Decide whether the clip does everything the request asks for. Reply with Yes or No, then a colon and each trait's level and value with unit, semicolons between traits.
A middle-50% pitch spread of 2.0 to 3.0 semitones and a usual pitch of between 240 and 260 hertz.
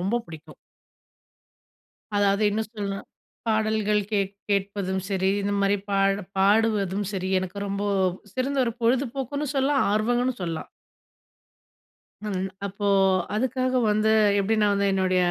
No: average, 2.7 semitones; high, 205 Hz